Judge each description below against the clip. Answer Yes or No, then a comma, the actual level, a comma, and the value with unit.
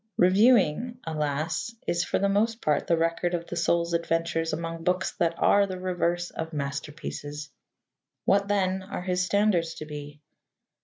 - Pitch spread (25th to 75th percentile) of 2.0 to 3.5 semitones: Yes, narrow, 2.6 semitones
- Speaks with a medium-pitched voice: Yes, medium, 170 Hz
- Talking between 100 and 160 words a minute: Yes, average, 155 wpm